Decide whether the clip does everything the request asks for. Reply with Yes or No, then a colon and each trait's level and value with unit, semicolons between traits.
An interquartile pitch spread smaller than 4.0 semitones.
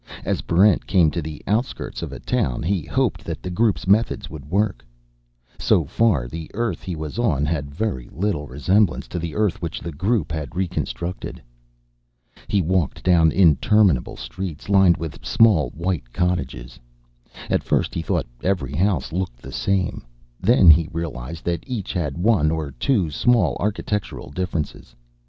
No: average, 4.5 semitones